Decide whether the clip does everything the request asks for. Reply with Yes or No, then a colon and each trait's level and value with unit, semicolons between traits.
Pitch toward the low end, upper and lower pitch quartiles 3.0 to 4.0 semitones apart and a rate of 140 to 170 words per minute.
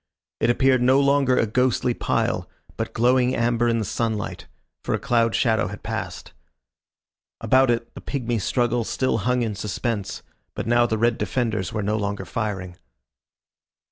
No: low, 115 Hz; narrow, 2.6 semitones; average, 160 wpm